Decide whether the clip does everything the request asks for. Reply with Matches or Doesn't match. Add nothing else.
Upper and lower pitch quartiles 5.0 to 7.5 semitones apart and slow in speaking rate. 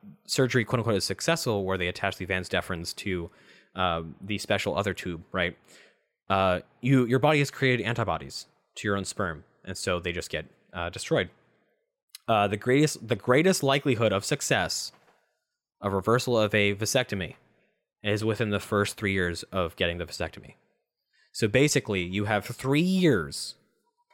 Doesn't match